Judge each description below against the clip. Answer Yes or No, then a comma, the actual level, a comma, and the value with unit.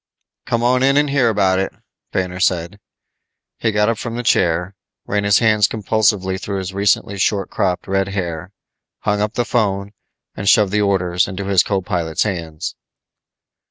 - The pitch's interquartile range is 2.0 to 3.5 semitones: Yes, narrow, 2.4 semitones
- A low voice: Yes, low, 100 Hz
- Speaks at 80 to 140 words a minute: No, average, 170 wpm